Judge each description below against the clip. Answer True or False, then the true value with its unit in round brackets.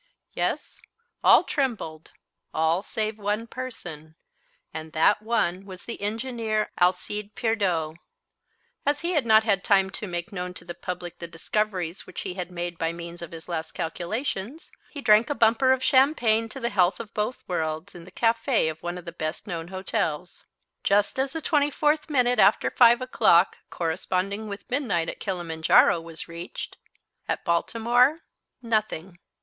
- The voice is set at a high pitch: True (200 Hz)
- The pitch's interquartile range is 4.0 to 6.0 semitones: True (5.2 semitones)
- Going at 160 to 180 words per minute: True (165 wpm)